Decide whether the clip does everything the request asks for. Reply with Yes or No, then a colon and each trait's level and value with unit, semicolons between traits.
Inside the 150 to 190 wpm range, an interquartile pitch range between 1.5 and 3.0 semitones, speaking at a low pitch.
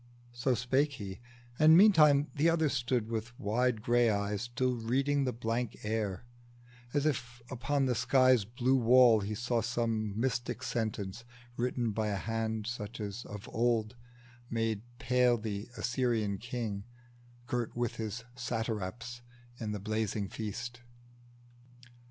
No: slow, 135 wpm; narrow, 2.5 semitones; low, 120 Hz